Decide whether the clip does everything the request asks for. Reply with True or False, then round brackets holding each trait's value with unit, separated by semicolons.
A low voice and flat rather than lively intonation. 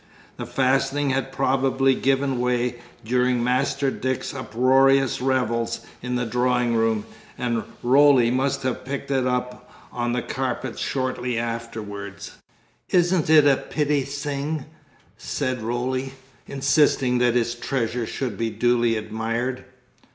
True (125 Hz; 2.1 semitones)